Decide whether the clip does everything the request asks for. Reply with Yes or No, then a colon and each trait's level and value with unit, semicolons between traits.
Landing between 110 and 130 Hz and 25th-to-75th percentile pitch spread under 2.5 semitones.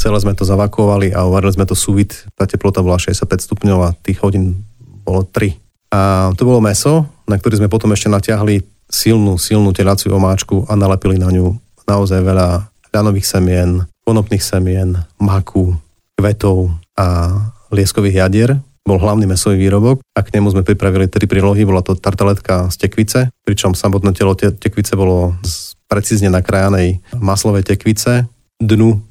No: low, 100 Hz; narrow, 2.0 semitones